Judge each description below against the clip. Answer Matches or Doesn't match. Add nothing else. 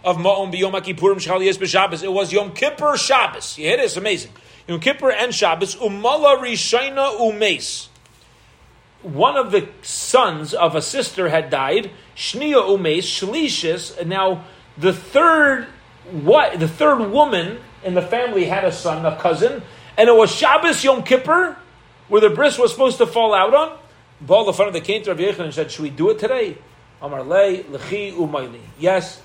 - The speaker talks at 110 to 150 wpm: Doesn't match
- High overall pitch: Matches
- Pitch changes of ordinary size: Doesn't match